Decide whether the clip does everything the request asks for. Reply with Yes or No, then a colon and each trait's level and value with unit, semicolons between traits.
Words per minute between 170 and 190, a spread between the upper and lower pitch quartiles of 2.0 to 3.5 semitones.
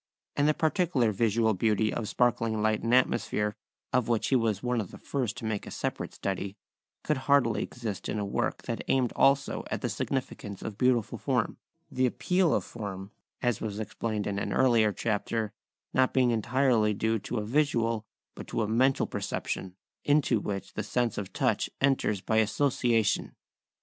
Yes: average, 175 wpm; average, 3.2 semitones